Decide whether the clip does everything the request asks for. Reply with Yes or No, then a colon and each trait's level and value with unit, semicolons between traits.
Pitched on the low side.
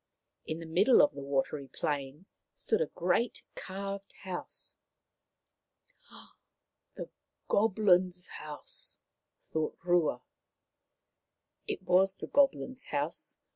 No: medium, 180 Hz